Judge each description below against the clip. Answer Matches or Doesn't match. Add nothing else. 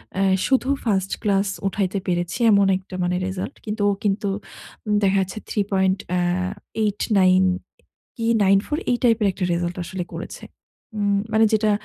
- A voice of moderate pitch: Doesn't match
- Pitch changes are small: Matches